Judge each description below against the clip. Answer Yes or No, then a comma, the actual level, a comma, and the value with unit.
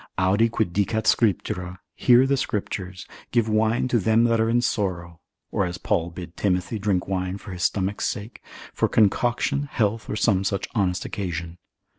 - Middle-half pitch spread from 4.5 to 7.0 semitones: No, average, 3.8 semitones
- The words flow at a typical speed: Yes, average, 170 wpm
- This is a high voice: No, low, 100 Hz